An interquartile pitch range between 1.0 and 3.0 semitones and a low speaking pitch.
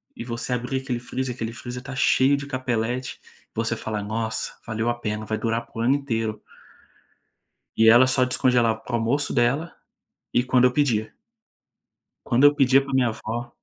Yes: narrow, 2.4 semitones; low, 120 Hz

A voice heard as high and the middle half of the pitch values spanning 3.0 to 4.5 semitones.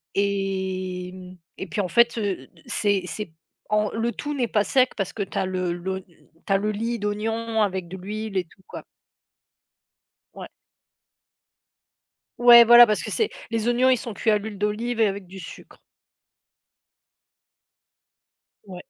Yes: high, 205 Hz; average, 3.3 semitones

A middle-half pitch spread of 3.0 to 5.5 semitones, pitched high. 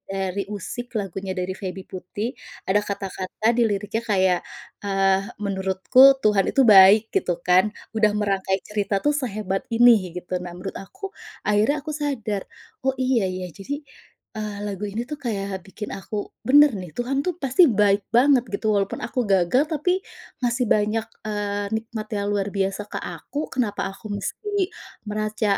Yes: average, 3.4 semitones; high, 205 Hz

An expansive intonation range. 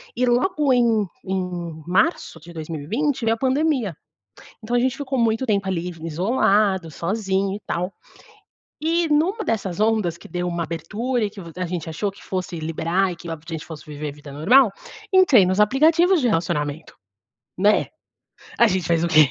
Yes: wide, 6.4 semitones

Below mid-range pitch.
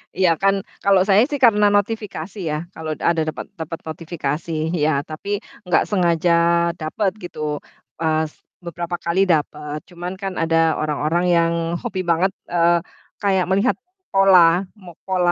No: medium, 175 Hz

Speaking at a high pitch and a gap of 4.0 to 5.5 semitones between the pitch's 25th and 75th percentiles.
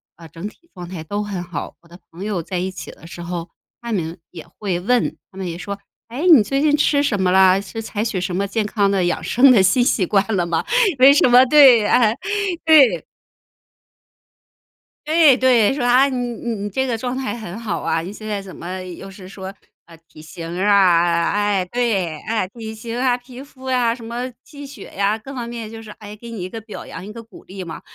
Yes: high, 210 Hz; average, 4.9 semitones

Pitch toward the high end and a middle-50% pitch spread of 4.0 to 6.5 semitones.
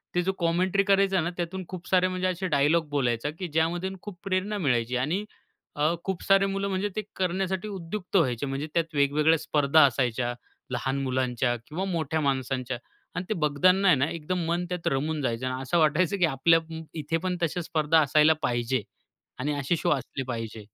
No: medium, 160 Hz; average, 5.3 semitones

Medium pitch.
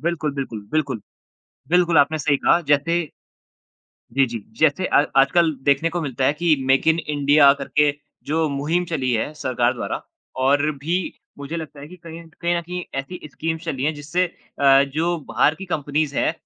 Yes: medium, 150 Hz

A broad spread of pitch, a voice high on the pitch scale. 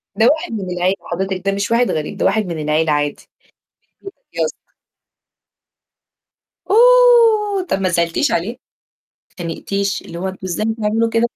Yes: wide, 5.8 semitones; high, 200 Hz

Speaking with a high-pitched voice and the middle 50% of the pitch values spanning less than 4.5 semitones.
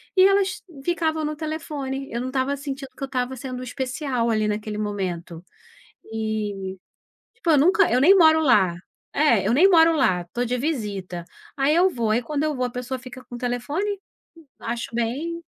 No: very high, 260 Hz; wide, 5.5 semitones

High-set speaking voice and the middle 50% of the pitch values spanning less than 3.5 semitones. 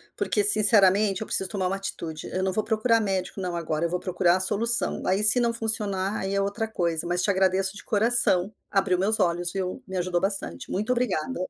Yes: high, 195 Hz; average, 2.8 semitones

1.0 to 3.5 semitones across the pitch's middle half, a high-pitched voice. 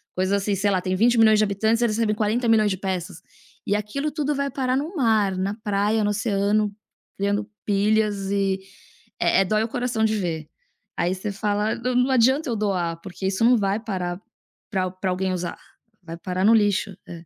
Yes: average, 2.8 semitones; high, 205 Hz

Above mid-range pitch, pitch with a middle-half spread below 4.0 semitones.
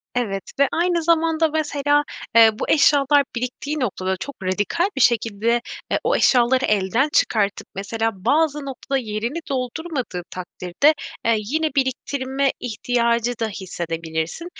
No: high, 245 Hz; wide, 5.5 semitones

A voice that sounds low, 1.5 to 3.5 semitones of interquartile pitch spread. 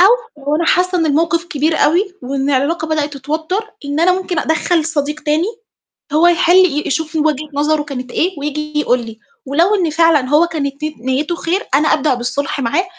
No: very high, 310 Hz; average, 2.9 semitones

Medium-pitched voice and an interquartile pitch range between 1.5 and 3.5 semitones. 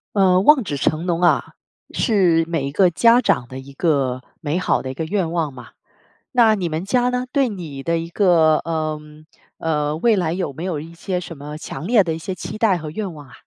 No: medium, 165 Hz; average, 4.0 semitones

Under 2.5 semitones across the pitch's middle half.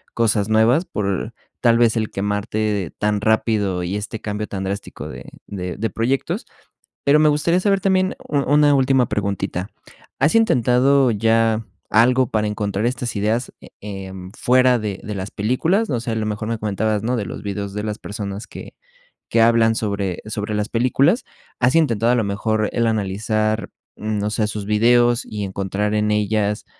No: average, 2.9 semitones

